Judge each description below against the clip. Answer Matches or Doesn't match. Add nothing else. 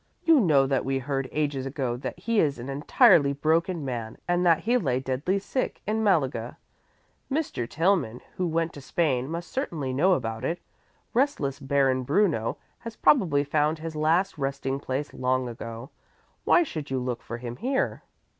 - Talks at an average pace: Matches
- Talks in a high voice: Doesn't match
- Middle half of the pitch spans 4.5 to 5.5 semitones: Matches